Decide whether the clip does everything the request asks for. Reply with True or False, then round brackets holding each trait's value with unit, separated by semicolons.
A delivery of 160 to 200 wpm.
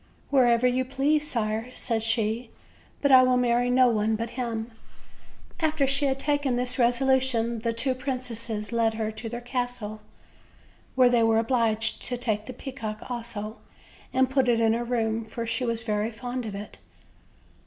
True (170 wpm)